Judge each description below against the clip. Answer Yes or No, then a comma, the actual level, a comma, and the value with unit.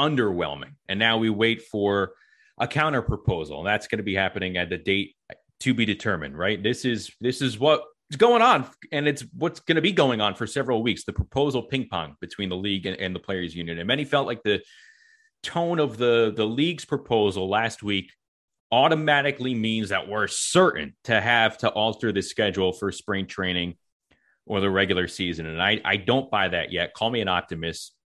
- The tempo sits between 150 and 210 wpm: Yes, average, 200 wpm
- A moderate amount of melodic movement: No, wide, 6.2 semitones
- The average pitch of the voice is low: Yes, low, 110 Hz